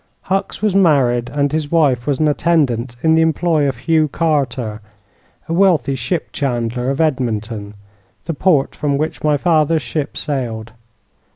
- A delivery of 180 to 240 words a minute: No, average, 155 wpm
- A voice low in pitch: No, medium, 145 Hz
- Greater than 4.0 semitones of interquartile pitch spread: Yes, average, 4.6 semitones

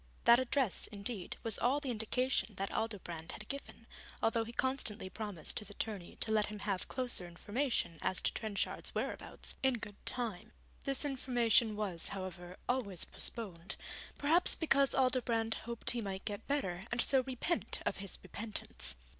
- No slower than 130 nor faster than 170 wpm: Yes, average, 155 wpm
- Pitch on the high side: Yes, high, 225 Hz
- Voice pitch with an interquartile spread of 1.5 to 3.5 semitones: No, average, 4.3 semitones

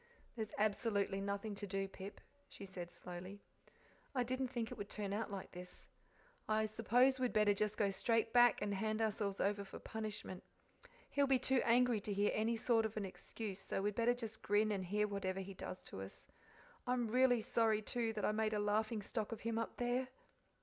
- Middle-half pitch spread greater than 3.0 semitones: No, narrow, 2.4 semitones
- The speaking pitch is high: Yes, high, 215 Hz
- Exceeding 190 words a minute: Yes, average, 200 wpm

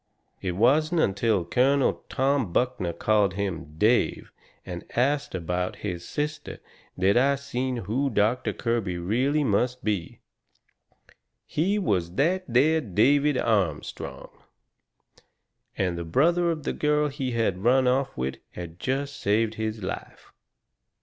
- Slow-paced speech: Yes, slow, 130 wpm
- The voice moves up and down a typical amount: No, wide, 6.7 semitones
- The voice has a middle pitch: No, low, 115 Hz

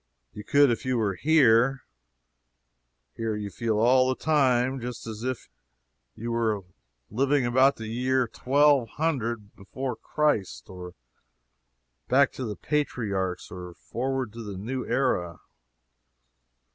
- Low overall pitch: Yes, low, 120 Hz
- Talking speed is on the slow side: Yes, slow, 125 wpm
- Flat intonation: No, average, 3.7 semitones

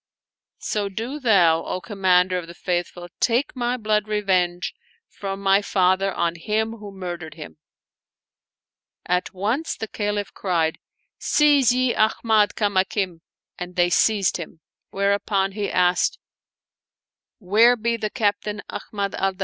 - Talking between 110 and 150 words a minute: Yes, average, 140 wpm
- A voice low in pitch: No, high, 200 Hz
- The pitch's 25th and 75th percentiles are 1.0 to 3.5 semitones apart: Yes, average, 3.2 semitones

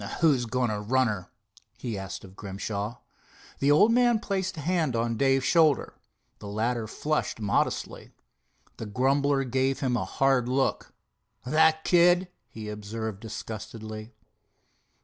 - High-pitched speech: No, low, 125 Hz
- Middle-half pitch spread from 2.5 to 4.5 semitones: No, average, 5.3 semitones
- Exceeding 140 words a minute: No, slow, 135 wpm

